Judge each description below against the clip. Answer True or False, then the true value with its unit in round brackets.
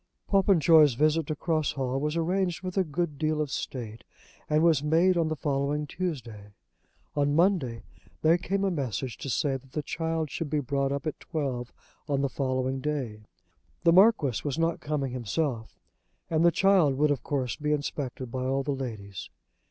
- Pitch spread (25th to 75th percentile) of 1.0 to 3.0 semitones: False (3.6 semitones)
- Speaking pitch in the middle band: True (145 Hz)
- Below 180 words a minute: False (185 wpm)